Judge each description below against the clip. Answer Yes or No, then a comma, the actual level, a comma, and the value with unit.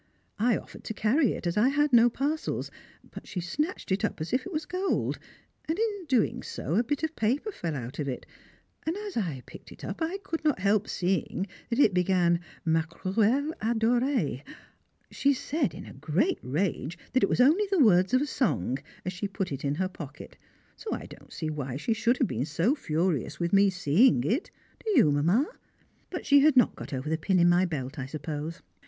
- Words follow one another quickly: Yes, fast, 210 wpm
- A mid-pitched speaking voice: No, high, 200 Hz